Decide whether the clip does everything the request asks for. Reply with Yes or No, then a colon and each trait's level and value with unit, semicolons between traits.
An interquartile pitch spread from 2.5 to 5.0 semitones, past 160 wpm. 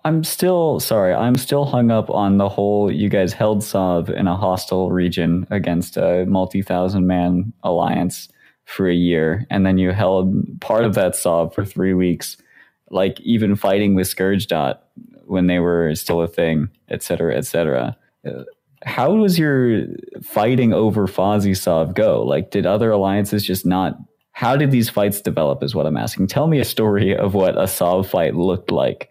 Yes: average, 3.3 semitones; average, 180 wpm